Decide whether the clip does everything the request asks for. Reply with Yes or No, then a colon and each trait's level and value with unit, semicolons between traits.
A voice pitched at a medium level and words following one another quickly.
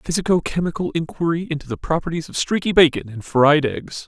No: medium, 160 Hz; average, 190 wpm